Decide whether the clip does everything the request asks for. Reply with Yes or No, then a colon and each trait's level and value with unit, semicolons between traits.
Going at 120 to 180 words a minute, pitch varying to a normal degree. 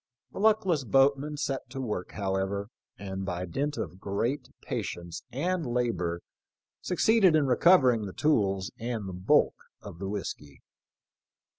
No: average, 140 wpm; wide, 7.1 semitones